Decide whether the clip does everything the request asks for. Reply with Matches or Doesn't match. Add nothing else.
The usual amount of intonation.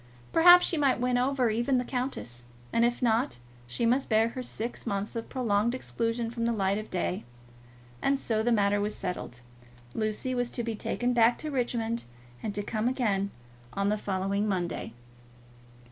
Matches